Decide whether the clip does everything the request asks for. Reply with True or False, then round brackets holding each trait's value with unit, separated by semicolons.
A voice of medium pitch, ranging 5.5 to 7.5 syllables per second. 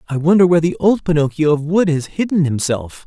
True (160 Hz; 5.9 syllables/s)